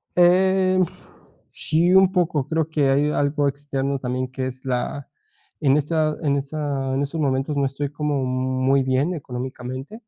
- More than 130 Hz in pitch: Yes, medium, 140 Hz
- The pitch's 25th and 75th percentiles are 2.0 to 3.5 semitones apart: Yes, average, 2.8 semitones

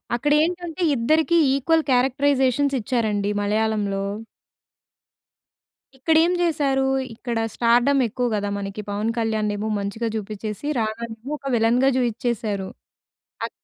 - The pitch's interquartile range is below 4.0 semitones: No, average, 4.4 semitones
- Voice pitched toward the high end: Yes, high, 235 Hz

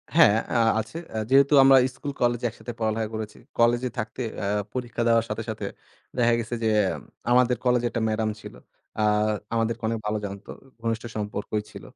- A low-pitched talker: Yes, low, 115 Hz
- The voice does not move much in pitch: Yes, narrow, 1.9 semitones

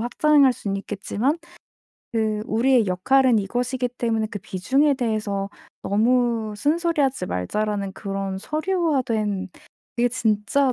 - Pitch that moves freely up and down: No, average, 4.5 semitones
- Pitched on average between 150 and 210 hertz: No, high, 225 Hz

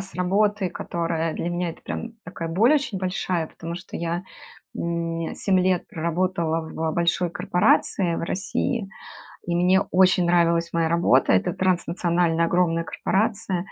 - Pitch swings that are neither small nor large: No, narrow, 1.9 semitones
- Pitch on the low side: No, medium, 175 Hz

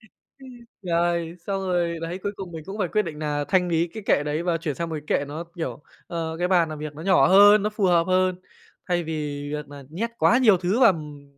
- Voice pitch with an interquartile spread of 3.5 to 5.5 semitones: No, average, 2.9 semitones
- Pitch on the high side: No, medium, 170 Hz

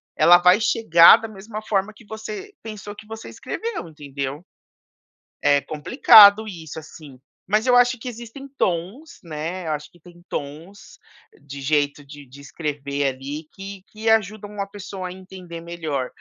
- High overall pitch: No, medium, 180 Hz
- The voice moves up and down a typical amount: No, wide, 6.2 semitones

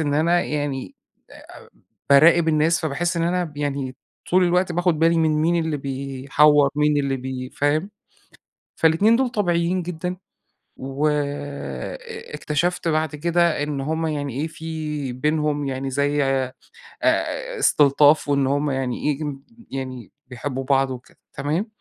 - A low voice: No, medium, 150 Hz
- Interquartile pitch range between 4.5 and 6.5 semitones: No, average, 3.2 semitones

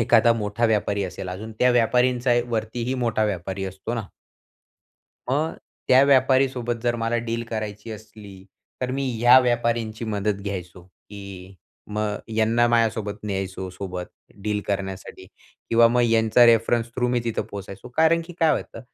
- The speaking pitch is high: No, low, 110 Hz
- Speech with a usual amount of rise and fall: Yes, average, 3.1 semitones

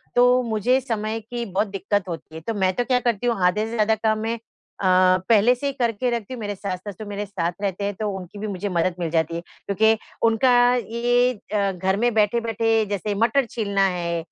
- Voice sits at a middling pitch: No, high, 210 Hz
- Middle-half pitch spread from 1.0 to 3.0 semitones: No, average, 3.4 semitones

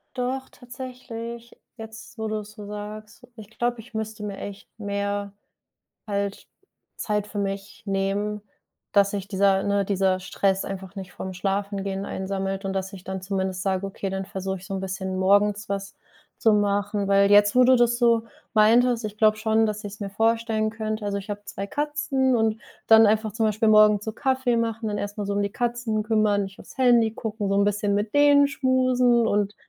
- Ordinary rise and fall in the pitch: No, narrow, 2.2 semitones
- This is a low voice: No, high, 210 Hz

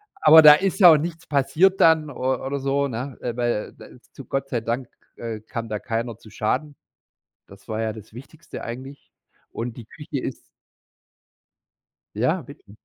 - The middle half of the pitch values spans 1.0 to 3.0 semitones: No, average, 4.5 semitones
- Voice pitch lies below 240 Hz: Yes, low, 135 Hz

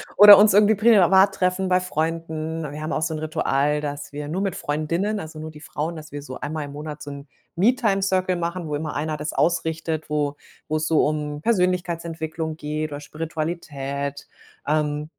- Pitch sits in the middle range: Yes, medium, 160 Hz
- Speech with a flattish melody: No, average, 3.2 semitones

